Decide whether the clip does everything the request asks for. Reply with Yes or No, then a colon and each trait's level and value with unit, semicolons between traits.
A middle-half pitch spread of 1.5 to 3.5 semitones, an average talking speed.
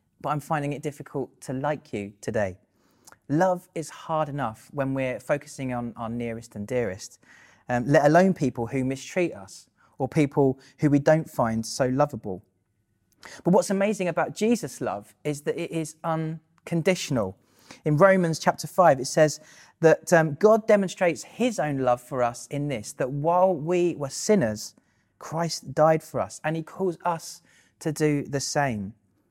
No: average, 4.4 semitones; average, 165 wpm